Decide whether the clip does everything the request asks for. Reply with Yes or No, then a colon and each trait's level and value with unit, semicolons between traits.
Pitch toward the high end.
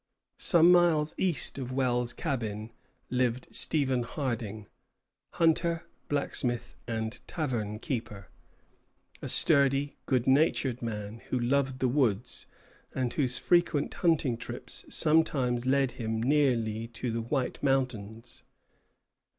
No: low, 130 Hz